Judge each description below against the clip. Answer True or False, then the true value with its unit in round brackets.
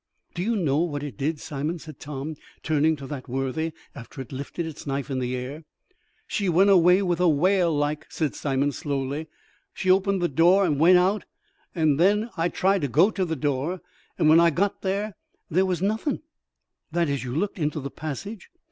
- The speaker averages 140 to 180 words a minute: False (200 wpm)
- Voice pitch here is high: False (160 Hz)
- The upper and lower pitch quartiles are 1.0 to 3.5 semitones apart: False (4.5 semitones)